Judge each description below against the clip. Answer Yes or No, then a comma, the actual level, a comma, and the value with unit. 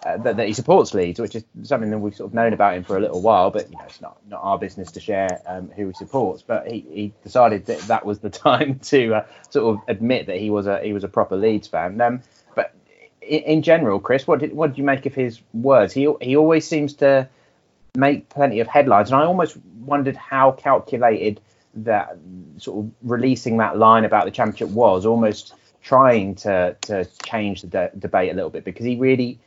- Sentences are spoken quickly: Yes, fast, 230 wpm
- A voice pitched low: Yes, low, 115 Hz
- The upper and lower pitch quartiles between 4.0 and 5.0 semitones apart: Yes, average, 4.7 semitones